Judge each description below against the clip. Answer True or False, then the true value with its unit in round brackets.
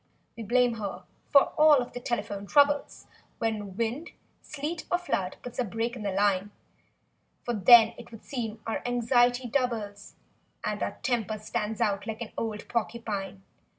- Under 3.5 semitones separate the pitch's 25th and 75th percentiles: True (2.9 semitones)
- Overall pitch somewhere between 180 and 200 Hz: False (230 Hz)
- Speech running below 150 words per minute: False (155 wpm)